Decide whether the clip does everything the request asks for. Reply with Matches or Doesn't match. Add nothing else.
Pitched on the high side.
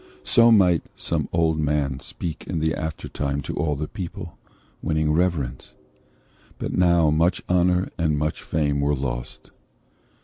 Doesn't match